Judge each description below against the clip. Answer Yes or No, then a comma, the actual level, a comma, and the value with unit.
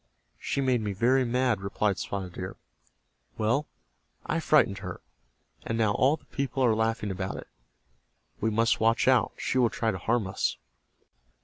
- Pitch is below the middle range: Yes, low, 115 Hz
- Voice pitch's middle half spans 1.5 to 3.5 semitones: No, average, 4.0 semitones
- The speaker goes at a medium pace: Yes, average, 165 wpm